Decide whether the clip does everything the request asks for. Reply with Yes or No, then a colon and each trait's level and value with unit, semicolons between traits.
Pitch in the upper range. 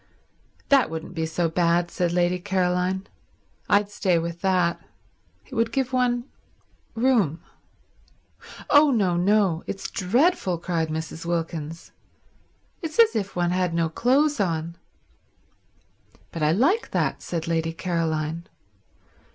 No: medium, 180 Hz